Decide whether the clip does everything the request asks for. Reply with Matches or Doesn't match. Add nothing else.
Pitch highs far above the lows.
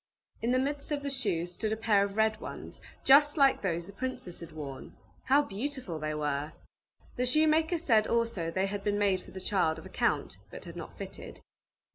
Matches